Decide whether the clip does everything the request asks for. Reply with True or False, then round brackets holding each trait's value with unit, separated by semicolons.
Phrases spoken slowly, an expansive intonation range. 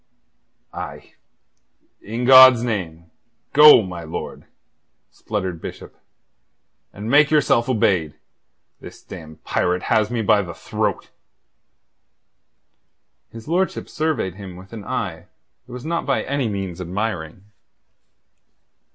True (110 wpm; 6.0 semitones)